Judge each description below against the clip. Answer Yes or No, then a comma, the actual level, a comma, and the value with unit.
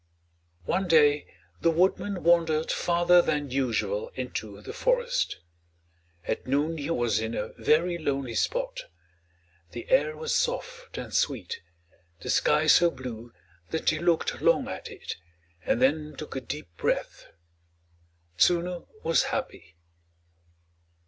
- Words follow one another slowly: Yes, slow, 130 wpm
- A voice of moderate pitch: Yes, medium, 155 Hz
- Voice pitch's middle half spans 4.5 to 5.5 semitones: Yes, average, 5.2 semitones